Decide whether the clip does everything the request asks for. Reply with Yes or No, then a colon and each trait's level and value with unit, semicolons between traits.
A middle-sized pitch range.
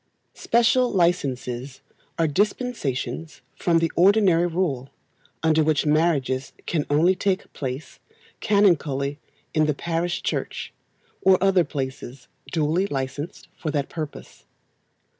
Yes: average, 4.5 semitones